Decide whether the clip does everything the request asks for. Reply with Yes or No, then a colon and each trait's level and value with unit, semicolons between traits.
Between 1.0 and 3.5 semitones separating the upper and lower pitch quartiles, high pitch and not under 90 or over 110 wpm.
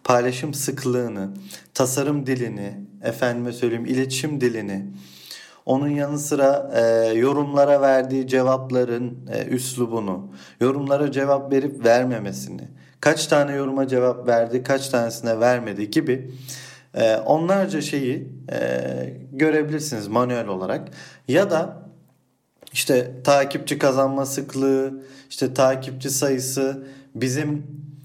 No: average, 3.0 semitones; low, 130 Hz; average, 100 wpm